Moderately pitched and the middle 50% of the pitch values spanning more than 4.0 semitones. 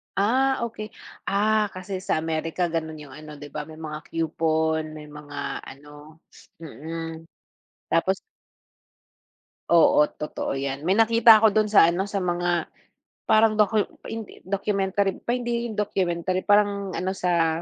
Yes: medium, 175 Hz; average, 4.6 semitones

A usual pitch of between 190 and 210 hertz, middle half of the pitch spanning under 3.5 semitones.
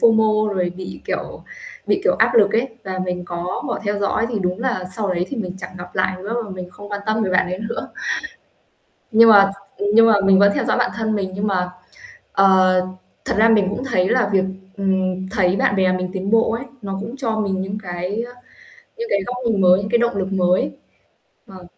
Yes: high, 200 Hz; average, 2.9 semitones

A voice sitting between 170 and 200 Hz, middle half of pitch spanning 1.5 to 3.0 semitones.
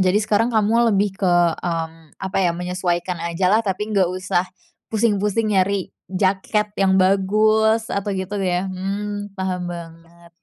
Yes: high, 190 Hz; narrow, 2.4 semitones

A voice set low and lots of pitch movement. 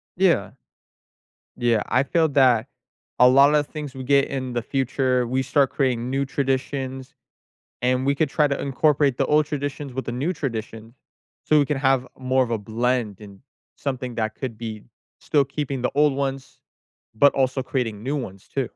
No: low, 130 Hz; narrow, 2.4 semitones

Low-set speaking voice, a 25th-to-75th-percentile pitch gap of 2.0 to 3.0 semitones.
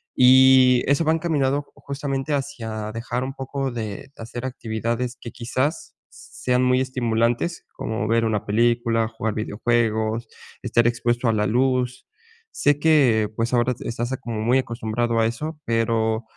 Yes: low, 120 Hz; narrow, 2.6 semitones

